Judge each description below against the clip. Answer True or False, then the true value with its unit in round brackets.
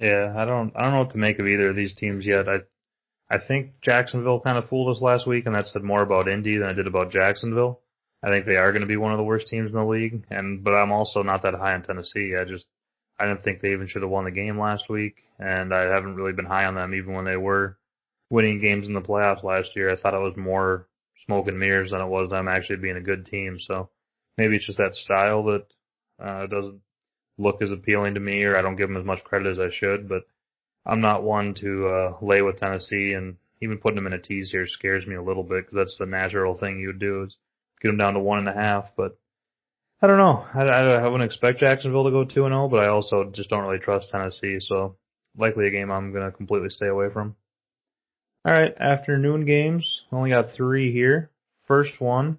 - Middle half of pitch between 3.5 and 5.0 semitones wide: False (2.6 semitones)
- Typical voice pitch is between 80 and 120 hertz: True (100 Hz)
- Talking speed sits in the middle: False (250 wpm)